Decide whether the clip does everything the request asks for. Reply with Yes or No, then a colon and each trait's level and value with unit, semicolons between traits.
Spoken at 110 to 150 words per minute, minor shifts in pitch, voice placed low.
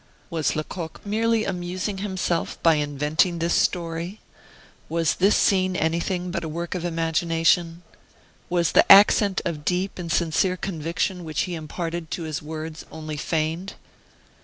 No: average, 140 wpm; narrow, 2.3 semitones; medium, 170 Hz